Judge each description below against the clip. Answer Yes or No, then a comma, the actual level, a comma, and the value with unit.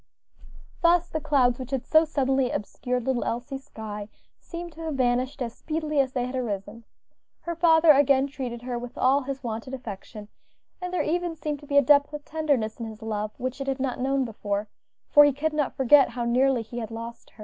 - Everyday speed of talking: No, fast, 210 wpm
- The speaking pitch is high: Yes, very high, 265 Hz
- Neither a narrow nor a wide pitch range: Yes, average, 3.7 semitones